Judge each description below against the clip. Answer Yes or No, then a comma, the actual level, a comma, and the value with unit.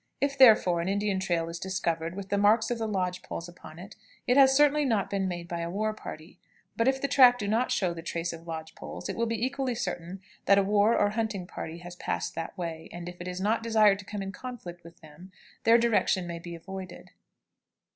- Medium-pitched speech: No, high, 195 Hz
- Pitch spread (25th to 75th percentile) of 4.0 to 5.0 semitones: Yes, average, 4.5 semitones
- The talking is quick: Yes, fast, 235 wpm